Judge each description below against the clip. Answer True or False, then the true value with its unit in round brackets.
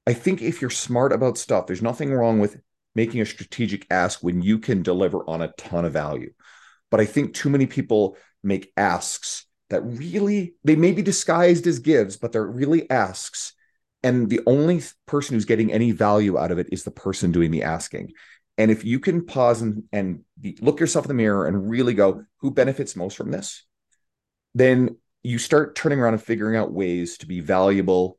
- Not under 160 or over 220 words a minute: True (200 wpm)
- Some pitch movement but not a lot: False (6.6 semitones)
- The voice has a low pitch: True (115 Hz)